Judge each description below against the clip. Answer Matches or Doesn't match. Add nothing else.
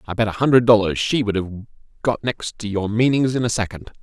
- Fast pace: Matches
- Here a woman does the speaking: Doesn't match